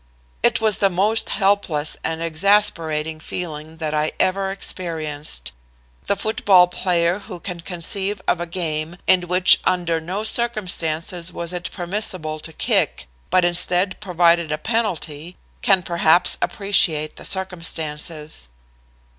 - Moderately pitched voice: Yes, medium, 175 Hz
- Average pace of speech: No, slow, 130 wpm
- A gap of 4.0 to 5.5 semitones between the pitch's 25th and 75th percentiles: No, average, 3.3 semitones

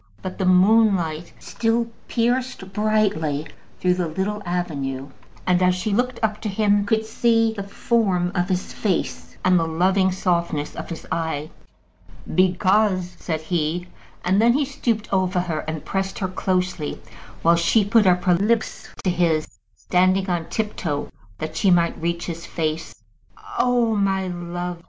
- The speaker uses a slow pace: No, average, 165 wpm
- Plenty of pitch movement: No, average, 3.5 semitones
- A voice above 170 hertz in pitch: Yes, medium, 185 Hz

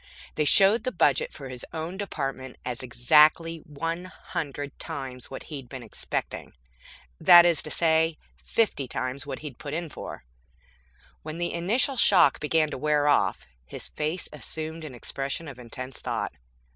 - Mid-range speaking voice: Yes, medium, 150 Hz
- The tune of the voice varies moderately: Yes, average, 3.7 semitones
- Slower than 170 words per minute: Yes, average, 160 wpm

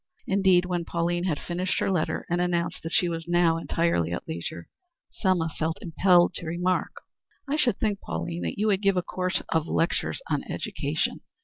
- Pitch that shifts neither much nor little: No, narrow, 2.2 semitones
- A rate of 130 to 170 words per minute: No, average, 185 wpm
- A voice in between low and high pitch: Yes, medium, 175 Hz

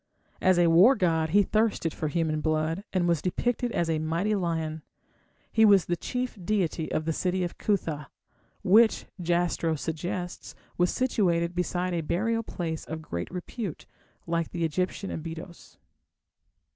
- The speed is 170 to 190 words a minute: No, average, 150 wpm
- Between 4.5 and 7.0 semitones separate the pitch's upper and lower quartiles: No, average, 2.9 semitones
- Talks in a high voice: No, medium, 175 Hz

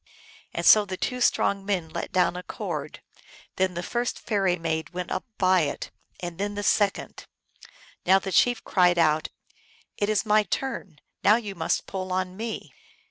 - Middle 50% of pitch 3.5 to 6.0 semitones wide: No, narrow, 2.5 semitones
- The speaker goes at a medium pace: Yes, average, 180 wpm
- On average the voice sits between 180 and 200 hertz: Yes, high, 190 Hz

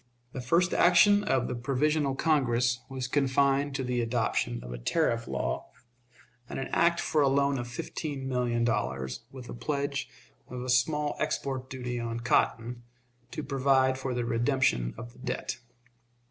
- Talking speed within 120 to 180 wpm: Yes, average, 160 wpm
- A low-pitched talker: Yes, low, 130 Hz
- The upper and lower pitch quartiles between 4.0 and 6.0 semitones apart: No, average, 2.8 semitones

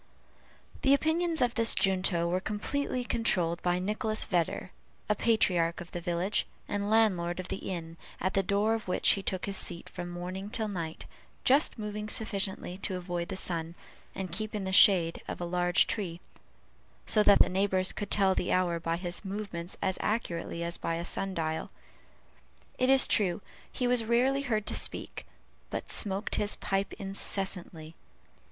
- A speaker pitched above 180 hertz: Yes, high, 190 Hz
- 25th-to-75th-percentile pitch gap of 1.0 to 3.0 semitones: No, average, 3.4 semitones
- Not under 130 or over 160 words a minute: No, average, 175 wpm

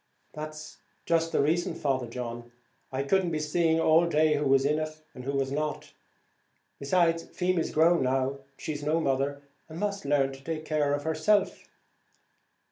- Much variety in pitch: No, average, 3.1 semitones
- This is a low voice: No, medium, 155 Hz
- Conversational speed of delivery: Yes, average, 160 wpm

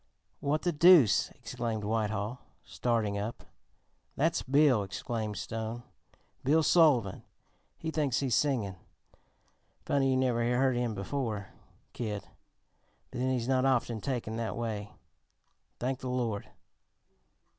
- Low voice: Yes, low, 120 Hz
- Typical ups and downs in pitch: Yes, average, 3.5 semitones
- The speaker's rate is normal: No, slow, 120 wpm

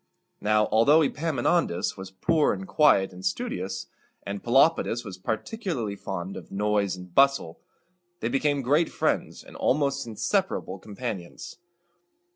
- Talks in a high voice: No, low, 110 Hz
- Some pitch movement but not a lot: No, wide, 6.7 semitones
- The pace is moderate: No, slow, 120 wpm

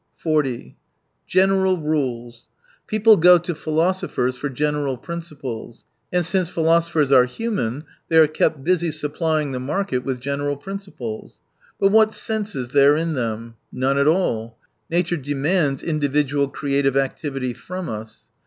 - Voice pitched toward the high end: No, medium, 150 Hz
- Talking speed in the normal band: Yes, average, 145 wpm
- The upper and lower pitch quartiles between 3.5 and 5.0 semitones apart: Yes, average, 4.6 semitones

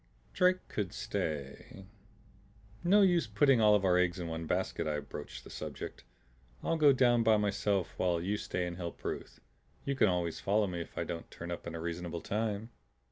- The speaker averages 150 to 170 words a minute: No, average, 190 wpm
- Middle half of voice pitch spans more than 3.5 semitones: Yes, average, 4.8 semitones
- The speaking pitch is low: Yes, very low, 95 Hz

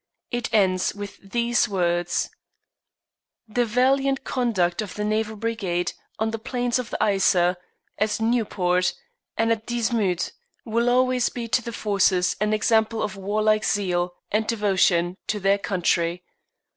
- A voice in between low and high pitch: No, high, 215 Hz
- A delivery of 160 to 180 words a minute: No, average, 140 wpm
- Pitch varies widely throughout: No, average, 3.7 semitones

